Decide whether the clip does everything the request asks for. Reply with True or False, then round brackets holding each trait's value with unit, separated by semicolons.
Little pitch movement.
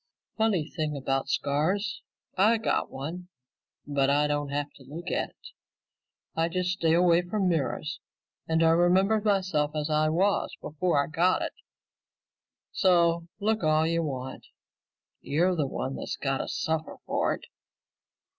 False (3.7 semitones)